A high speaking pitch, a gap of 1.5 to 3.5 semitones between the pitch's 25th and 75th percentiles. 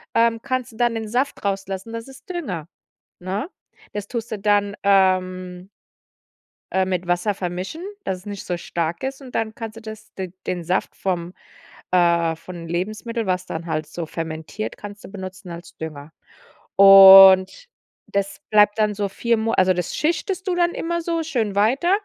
No: high, 195 Hz; average, 4.0 semitones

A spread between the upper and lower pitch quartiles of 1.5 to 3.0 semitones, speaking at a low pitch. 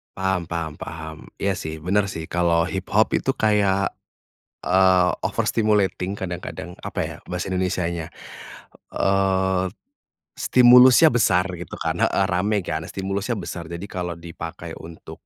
Yes: narrow, 2.4 semitones; very low, 95 Hz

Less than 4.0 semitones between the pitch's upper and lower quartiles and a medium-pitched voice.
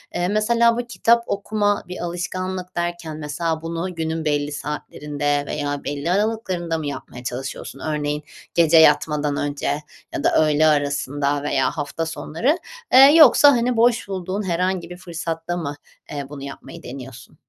No: average, 4.3 semitones; medium, 165 Hz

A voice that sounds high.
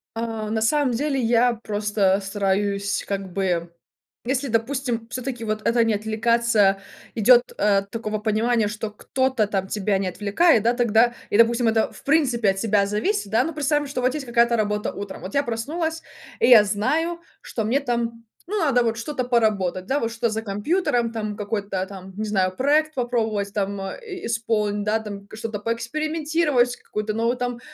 Yes: high, 225 Hz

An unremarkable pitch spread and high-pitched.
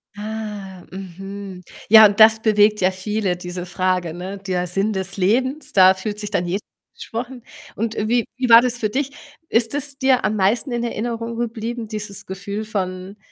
Yes: average, 3.3 semitones; high, 210 Hz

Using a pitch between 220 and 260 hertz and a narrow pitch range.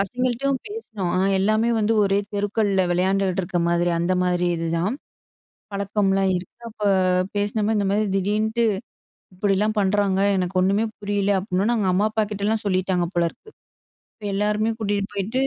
No: high, 200 Hz; narrow, 2.3 semitones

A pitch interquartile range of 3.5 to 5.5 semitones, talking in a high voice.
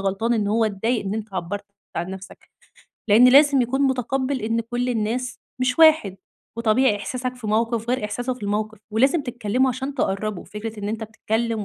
No: average, 3.1 semitones; high, 225 Hz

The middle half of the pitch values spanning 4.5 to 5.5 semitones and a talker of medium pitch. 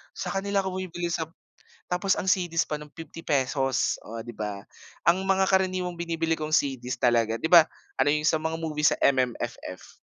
Yes: average, 5.0 semitones; medium, 160 Hz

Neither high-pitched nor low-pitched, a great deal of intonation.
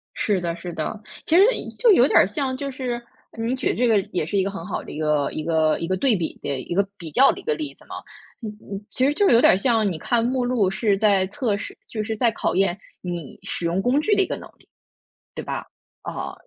No: high, 210 Hz; wide, 6.0 semitones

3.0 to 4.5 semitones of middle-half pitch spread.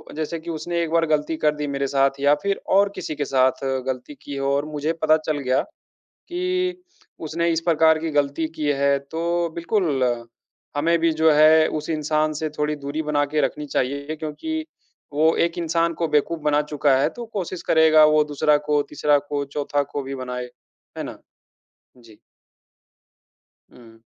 No: narrow, 2.4 semitones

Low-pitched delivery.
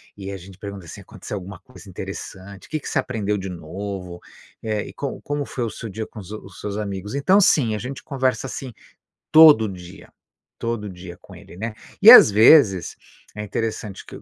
Yes: low, 105 Hz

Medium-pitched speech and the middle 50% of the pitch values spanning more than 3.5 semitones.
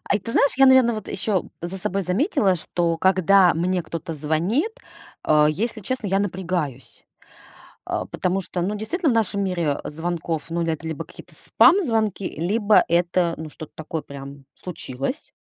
Yes: medium, 180 Hz; average, 4.5 semitones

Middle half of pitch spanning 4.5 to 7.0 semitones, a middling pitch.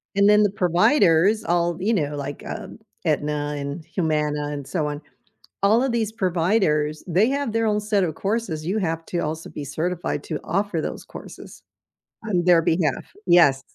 Yes: average, 5.2 semitones; medium, 170 Hz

